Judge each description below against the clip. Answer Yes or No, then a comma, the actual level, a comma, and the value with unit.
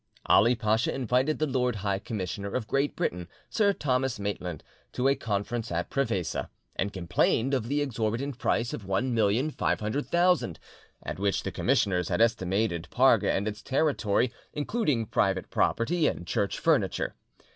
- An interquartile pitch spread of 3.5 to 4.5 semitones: No, average, 5.2 semitones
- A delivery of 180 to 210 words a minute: No, average, 145 wpm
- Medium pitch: No, low, 115 Hz